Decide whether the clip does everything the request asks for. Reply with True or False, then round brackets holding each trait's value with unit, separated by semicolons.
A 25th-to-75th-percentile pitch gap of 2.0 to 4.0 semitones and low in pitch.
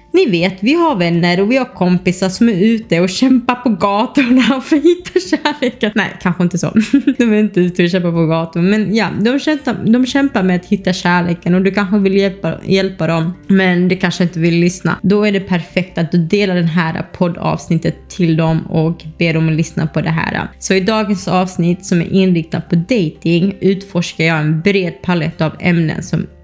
False (3.7 semitones; 185 Hz)